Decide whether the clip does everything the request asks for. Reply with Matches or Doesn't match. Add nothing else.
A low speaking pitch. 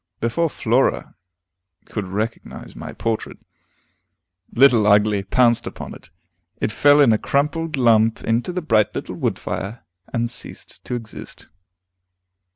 Matches